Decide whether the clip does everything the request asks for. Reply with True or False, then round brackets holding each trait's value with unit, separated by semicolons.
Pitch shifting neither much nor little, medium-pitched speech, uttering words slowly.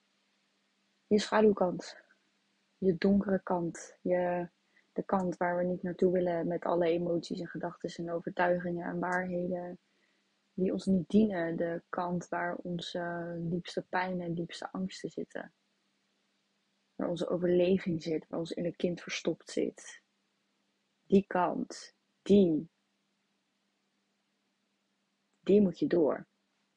False (1.5 semitones; 180 Hz; 120 wpm)